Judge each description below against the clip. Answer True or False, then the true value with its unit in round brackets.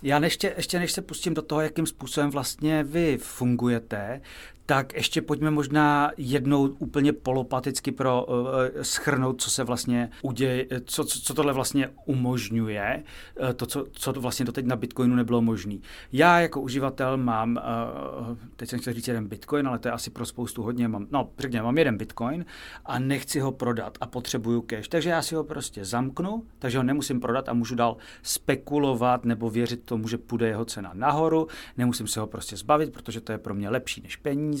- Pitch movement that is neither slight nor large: True (3.5 semitones)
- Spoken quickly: True (190 wpm)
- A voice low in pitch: True (130 Hz)